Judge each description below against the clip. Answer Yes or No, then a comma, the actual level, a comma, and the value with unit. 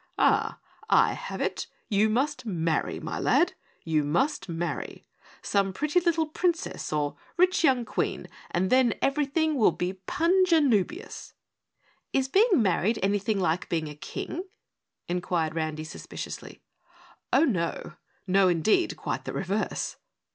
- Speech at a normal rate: No, slow, 130 wpm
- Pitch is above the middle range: Yes, high, 210 Hz